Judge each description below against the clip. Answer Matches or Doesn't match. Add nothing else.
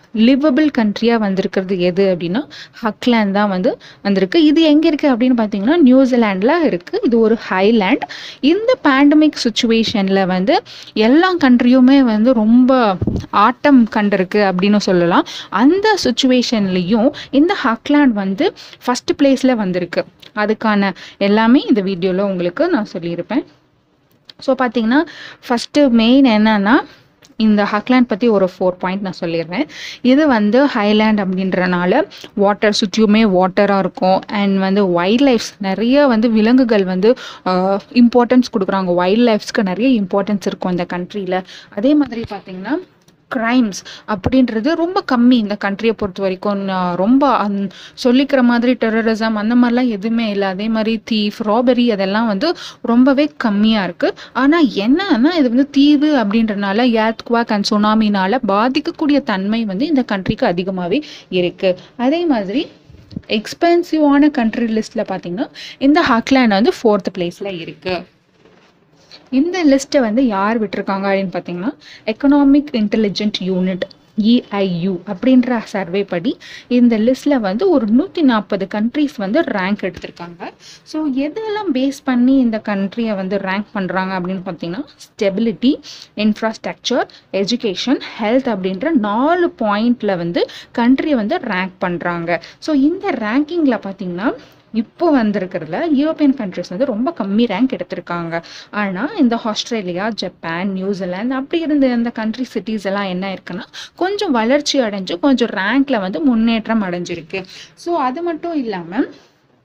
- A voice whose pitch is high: Matches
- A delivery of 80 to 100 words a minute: Doesn't match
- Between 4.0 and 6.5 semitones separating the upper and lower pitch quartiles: Matches